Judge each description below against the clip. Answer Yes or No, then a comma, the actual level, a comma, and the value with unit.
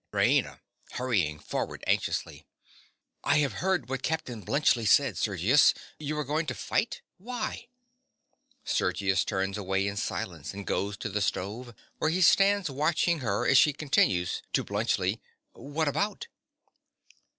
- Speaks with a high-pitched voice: No, low, 130 Hz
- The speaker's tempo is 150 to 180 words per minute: No, average, 140 wpm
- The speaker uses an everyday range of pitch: No, wide, 7.7 semitones